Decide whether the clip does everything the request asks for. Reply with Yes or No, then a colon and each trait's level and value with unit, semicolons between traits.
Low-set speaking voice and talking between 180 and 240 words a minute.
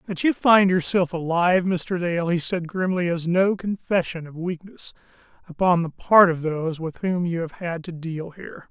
No: medium, 175 Hz; average, 195 wpm